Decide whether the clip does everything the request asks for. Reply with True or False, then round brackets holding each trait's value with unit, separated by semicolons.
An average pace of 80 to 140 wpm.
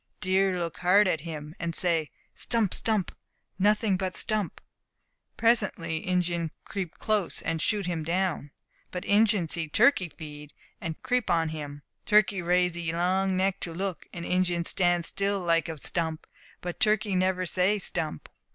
False (155 wpm)